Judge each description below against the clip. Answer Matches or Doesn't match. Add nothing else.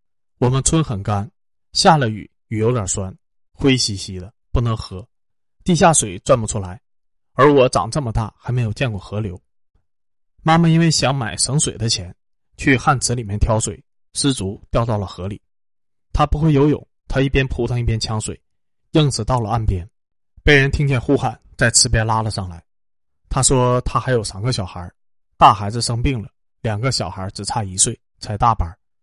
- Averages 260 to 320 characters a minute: Doesn't match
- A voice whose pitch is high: Doesn't match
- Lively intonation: Doesn't match